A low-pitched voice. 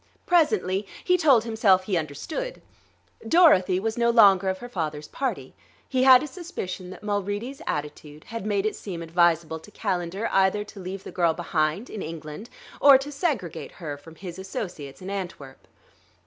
No: high, 190 Hz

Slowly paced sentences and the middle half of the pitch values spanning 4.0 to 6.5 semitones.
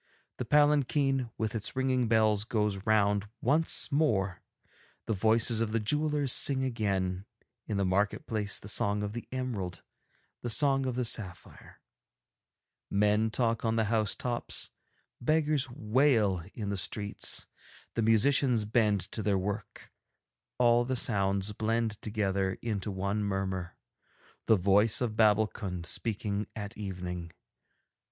No: slow, 130 wpm; average, 3.2 semitones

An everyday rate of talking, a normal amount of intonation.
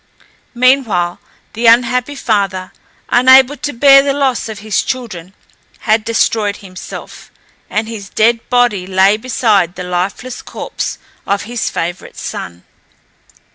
No: slow, 125 wpm; average, 4.5 semitones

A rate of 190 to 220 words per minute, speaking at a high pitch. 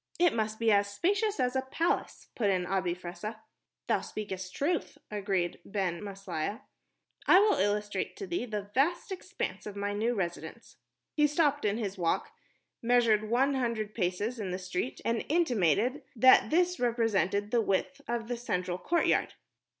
No: average, 160 wpm; high, 220 Hz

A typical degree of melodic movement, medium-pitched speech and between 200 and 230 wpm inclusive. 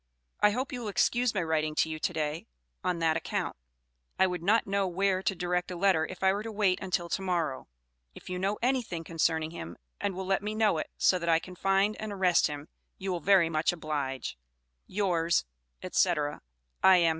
Yes: average, 3.3 semitones; medium, 180 Hz; fast, 205 wpm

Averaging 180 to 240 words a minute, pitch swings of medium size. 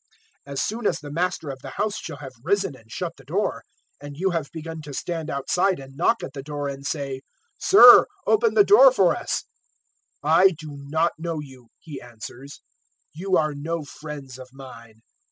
Yes: average, 190 wpm; average, 4.1 semitones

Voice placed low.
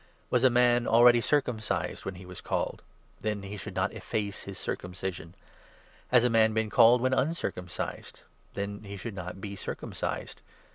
Yes: low, 105 Hz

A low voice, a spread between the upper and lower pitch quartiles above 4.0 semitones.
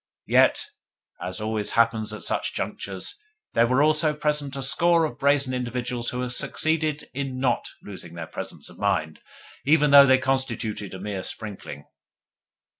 Yes: low, 125 Hz; average, 4.9 semitones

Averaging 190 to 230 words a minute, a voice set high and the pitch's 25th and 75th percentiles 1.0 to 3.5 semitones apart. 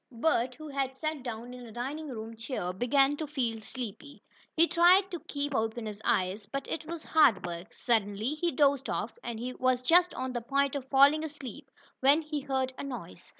No: average, 200 wpm; very high, 260 Hz; average, 4.2 semitones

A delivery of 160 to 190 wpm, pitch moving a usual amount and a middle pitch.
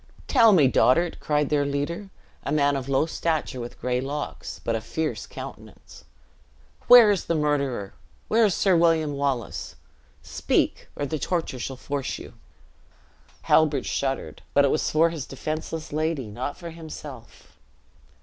No: average, 150 wpm; average, 3.4 semitones; medium, 150 Hz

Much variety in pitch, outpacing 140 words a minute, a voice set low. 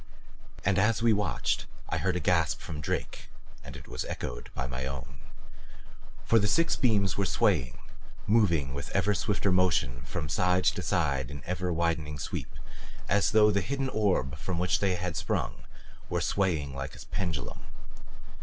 Yes: wide, 5.9 semitones; average, 165 wpm; very low, 90 Hz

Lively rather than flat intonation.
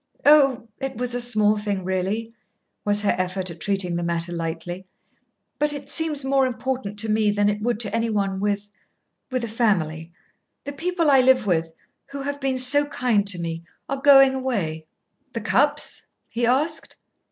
Yes: wide, 5.8 semitones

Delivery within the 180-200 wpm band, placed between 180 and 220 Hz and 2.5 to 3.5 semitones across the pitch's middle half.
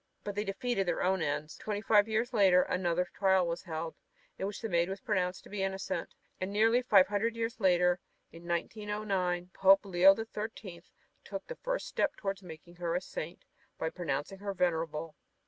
Yes: average, 190 wpm; high, 190 Hz; average, 3.0 semitones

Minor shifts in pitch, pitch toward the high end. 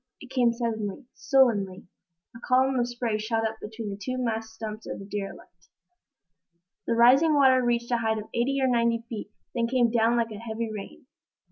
Yes: narrow, 2.3 semitones; high, 230 Hz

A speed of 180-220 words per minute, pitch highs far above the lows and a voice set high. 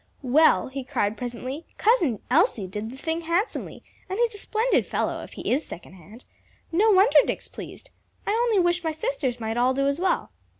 Yes: average, 190 wpm; wide, 8.3 semitones; very high, 315 Hz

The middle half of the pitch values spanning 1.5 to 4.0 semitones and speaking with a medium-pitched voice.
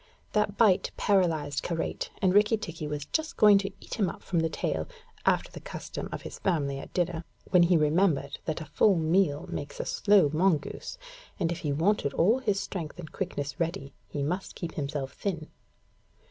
No: average, 4.7 semitones; medium, 170 Hz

